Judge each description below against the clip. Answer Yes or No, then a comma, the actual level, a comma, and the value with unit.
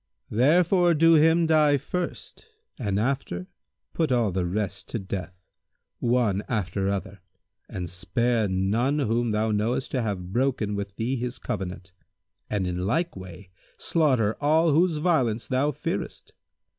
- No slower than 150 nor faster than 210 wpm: No, average, 140 wpm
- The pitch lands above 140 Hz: No, low, 115 Hz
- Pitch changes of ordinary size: No, wide, 6.8 semitones